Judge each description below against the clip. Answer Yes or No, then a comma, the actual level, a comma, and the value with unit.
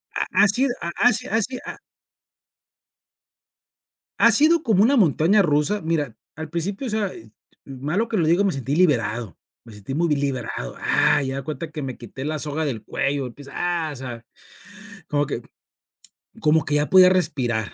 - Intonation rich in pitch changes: Yes, wide, 6.6 semitones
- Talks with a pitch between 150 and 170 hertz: Yes, medium, 155 Hz